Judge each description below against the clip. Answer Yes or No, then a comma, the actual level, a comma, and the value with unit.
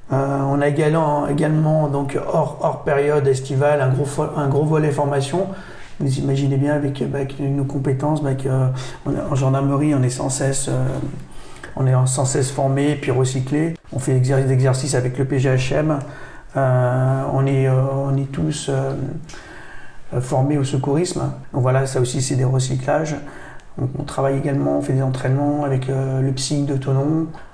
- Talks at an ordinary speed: Yes, average, 160 wpm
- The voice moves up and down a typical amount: No, narrow, 1.7 semitones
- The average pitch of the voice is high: No, medium, 140 Hz